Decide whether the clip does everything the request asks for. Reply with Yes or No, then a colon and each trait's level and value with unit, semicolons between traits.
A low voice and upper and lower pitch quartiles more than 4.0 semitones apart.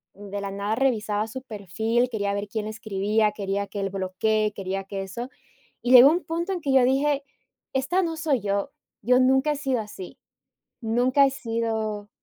No: high, 220 Hz; average, 4.6 semitones